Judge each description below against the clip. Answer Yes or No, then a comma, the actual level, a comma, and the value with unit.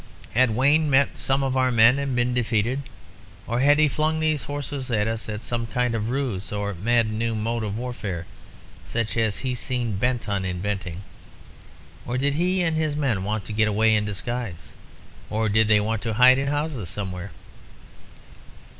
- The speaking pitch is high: No, low, 115 Hz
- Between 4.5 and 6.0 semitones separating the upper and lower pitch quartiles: No, average, 4.0 semitones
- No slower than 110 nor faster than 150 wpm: No, average, 180 wpm